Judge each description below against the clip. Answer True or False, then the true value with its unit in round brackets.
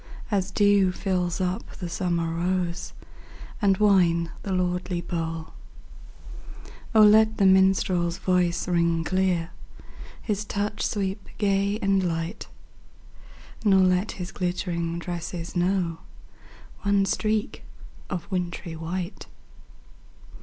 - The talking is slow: True (105 wpm)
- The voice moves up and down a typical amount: False (2.3 semitones)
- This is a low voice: False (185 Hz)